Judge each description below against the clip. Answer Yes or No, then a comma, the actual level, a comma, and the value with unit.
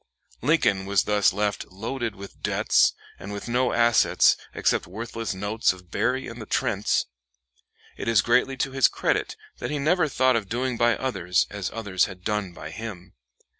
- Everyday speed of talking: Yes, average, 170 wpm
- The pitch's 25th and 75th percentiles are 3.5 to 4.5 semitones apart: Yes, average, 3.9 semitones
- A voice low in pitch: Yes, low, 110 Hz